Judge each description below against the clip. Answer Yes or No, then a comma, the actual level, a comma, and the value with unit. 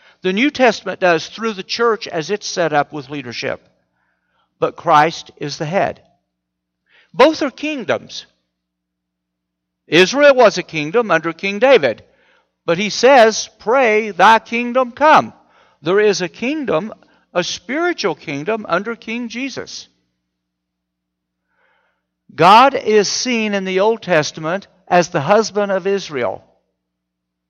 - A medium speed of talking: No, slow, 125 wpm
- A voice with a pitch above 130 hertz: Yes, medium, 185 Hz